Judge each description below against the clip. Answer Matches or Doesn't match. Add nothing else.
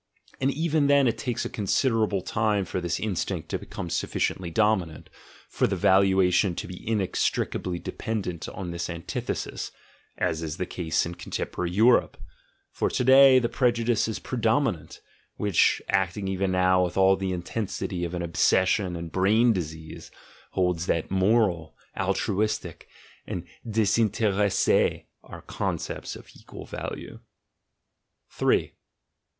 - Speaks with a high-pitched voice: Doesn't match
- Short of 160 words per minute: Matches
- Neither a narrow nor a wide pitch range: Matches